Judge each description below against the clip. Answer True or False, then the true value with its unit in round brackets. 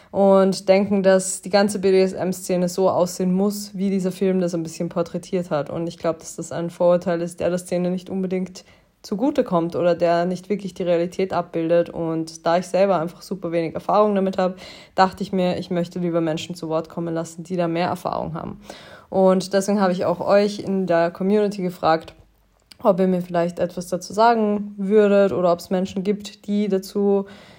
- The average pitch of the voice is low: False (185 Hz)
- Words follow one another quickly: True (195 wpm)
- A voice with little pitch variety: True (2.3 semitones)